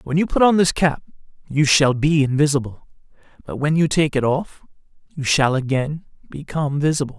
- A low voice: No, medium, 145 Hz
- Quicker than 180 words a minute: No, average, 175 wpm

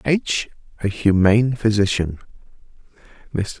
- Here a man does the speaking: Yes, male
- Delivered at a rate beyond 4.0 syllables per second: Yes, 4.6 syllables/s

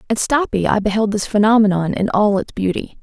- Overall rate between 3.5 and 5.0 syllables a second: No, 5.7 syllables/s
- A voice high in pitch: Yes, high, 210 Hz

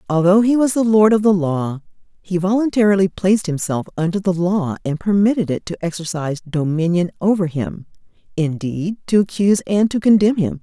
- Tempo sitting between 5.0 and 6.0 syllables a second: Yes, 5.4 syllables/s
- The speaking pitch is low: No, medium, 185 Hz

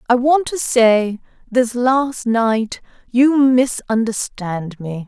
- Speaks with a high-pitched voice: Yes, high, 235 Hz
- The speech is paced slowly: Yes, slow, 95 wpm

